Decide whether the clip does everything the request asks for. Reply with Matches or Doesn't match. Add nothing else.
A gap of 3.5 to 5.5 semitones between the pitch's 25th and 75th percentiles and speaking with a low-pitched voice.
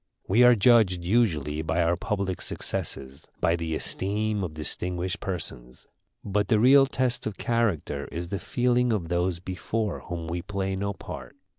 Matches